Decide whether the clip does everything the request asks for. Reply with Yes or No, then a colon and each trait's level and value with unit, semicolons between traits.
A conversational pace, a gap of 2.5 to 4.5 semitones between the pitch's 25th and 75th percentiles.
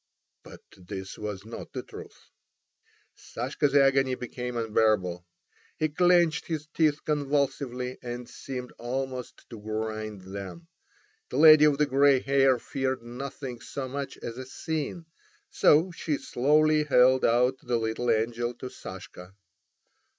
No: slow, 130 wpm; average, 3.8 semitones